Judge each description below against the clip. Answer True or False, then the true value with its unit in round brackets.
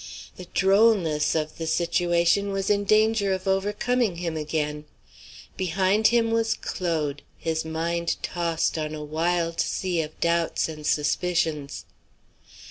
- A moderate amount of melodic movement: True (3.5 semitones)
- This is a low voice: False (170 Hz)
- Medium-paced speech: False (130 wpm)